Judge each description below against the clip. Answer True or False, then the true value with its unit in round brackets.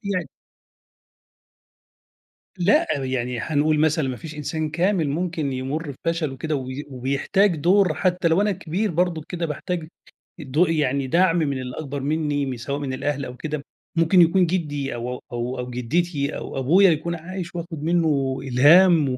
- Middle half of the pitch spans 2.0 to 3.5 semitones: False (4.2 semitones)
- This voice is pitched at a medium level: True (155 Hz)